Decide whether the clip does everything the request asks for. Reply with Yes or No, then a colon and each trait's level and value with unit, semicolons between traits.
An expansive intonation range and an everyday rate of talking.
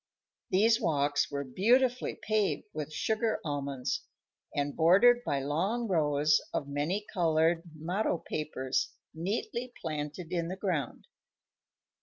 No: wide, 6.1 semitones; slow, 115 wpm